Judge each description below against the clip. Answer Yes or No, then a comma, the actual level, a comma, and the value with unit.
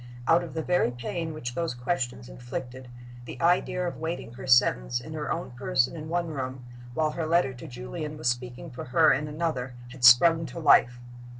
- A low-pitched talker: Yes, low, 130 Hz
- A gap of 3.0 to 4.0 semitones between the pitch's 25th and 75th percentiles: No, average, 4.9 semitones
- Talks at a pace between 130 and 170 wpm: No, average, 195 wpm